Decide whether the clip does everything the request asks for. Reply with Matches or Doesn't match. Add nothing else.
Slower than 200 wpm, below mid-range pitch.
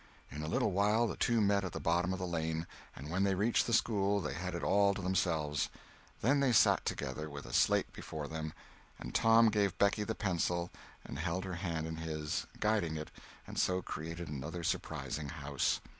Doesn't match